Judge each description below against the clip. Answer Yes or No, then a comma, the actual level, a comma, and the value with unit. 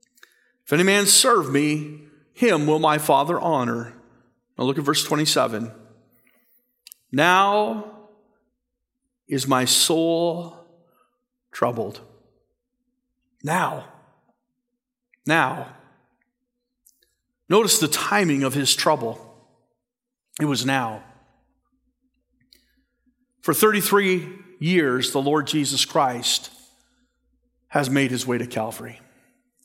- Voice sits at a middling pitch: Yes, medium, 180 Hz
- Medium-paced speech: No, slow, 90 wpm